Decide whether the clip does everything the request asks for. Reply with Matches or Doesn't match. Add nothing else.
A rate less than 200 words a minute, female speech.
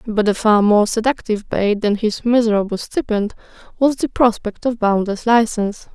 Matches